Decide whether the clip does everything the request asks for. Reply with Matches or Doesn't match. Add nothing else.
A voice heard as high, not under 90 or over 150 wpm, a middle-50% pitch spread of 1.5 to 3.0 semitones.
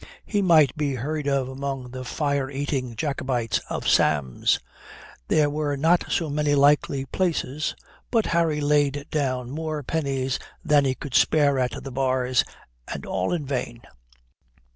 Doesn't match